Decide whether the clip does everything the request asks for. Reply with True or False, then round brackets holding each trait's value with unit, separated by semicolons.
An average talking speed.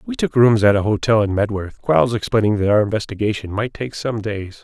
False (220 wpm)